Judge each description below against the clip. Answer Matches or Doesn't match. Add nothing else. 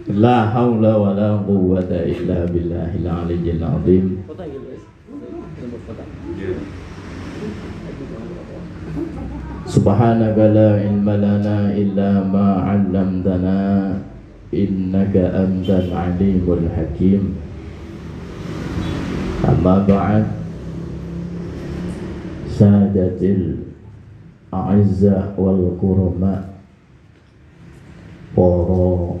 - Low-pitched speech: Matches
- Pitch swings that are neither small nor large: Doesn't match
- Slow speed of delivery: Matches